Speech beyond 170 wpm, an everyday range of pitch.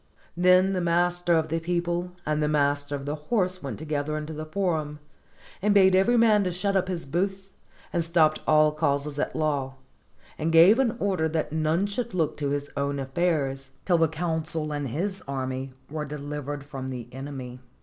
Yes: average, 185 wpm; average, 3.9 semitones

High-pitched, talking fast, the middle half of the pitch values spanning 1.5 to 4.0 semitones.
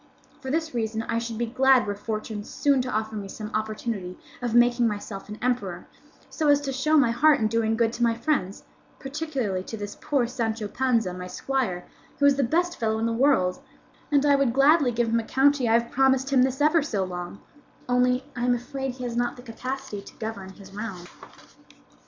Yes: high, 240 Hz; fast, 210 wpm; average, 3.6 semitones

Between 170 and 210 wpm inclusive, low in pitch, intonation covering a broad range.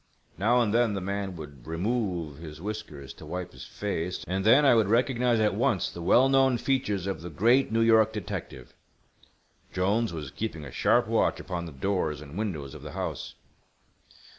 Yes: average, 185 wpm; low, 100 Hz; wide, 5.9 semitones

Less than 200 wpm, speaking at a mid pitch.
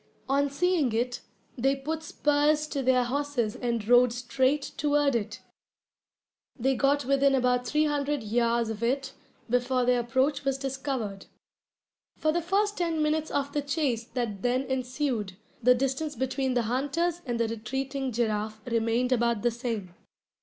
No: average, 155 wpm; very high, 260 Hz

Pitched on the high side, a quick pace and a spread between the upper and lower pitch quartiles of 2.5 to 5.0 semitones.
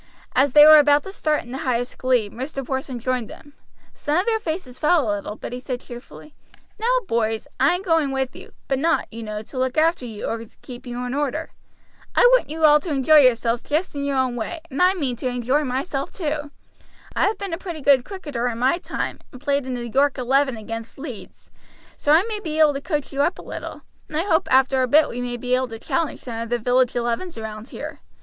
Yes: very high, 270 Hz; fast, 240 wpm; average, 4.0 semitones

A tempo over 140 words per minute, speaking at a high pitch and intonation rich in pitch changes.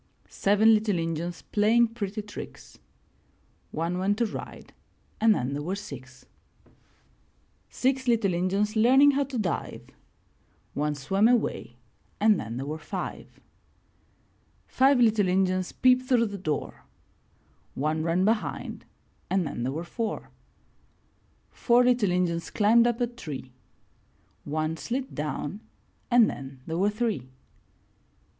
No: slow, 135 wpm; high, 200 Hz; wide, 6.3 semitones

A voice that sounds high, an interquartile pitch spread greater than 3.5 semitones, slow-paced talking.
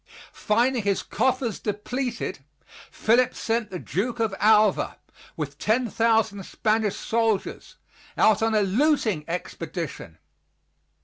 No: high, 220 Hz; average, 2.8 semitones; slow, 105 wpm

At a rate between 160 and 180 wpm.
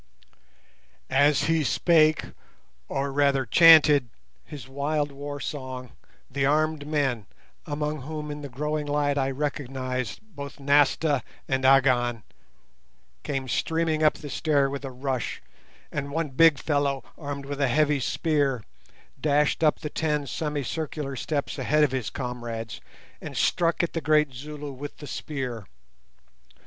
No: slow, 135 wpm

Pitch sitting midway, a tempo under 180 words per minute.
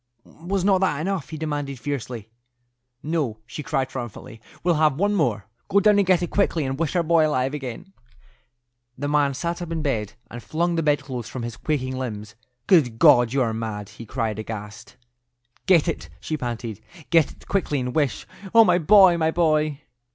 No: medium, 145 Hz; average, 185 wpm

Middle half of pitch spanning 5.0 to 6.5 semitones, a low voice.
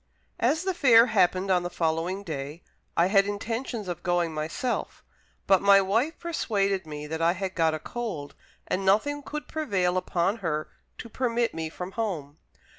No: wide, 5.4 semitones; high, 190 Hz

